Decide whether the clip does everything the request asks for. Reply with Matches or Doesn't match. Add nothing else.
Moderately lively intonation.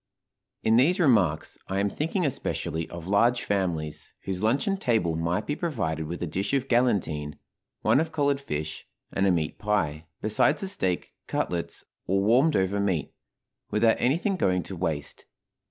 Doesn't match